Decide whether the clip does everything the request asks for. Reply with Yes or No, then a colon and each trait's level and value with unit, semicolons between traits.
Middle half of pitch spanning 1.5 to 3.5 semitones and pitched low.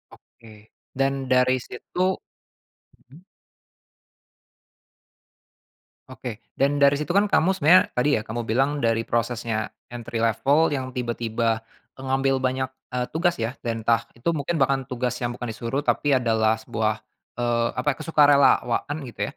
Yes: average, 3.2 semitones; low, 125 Hz